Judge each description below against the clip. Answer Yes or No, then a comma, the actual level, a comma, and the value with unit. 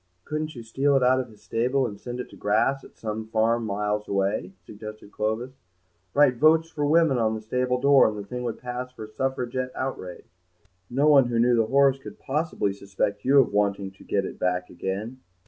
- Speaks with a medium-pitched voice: No, low, 120 Hz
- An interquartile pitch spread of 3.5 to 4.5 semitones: Yes, average, 4.0 semitones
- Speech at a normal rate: No, fast, 210 wpm